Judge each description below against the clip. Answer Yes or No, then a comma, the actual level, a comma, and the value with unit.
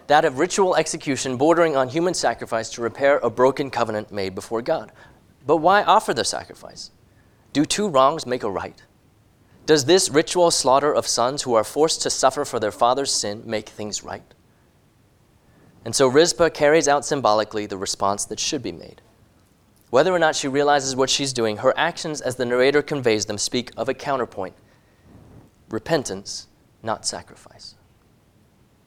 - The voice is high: No, low, 120 Hz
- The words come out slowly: No, average, 165 wpm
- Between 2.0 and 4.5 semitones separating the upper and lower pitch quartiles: No, average, 5.3 semitones